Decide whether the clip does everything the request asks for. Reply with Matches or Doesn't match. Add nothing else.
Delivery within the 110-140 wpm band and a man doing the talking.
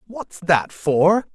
Matches